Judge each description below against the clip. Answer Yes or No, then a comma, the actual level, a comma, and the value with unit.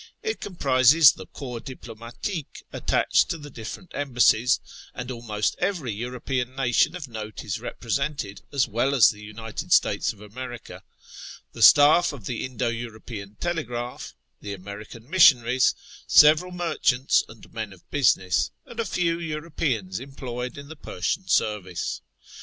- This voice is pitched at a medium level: No, low, 125 Hz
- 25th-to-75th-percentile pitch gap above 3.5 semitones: Yes, average, 4.7 semitones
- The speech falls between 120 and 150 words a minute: Yes, average, 140 wpm